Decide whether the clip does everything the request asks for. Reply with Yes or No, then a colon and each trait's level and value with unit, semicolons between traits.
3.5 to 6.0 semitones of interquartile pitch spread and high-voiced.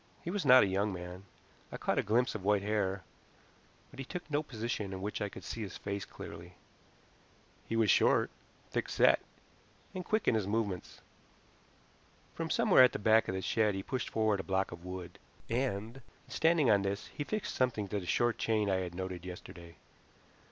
No: average, 3.8 semitones; low, 105 Hz